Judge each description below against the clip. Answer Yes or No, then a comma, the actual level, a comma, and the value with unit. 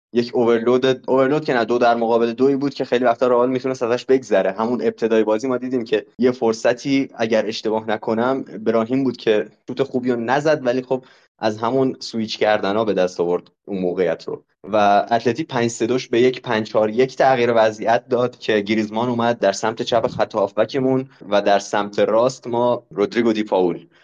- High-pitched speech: No, low, 120 Hz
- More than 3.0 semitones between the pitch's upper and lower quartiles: No, average, 2.7 semitones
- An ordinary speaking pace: No, fast, 185 wpm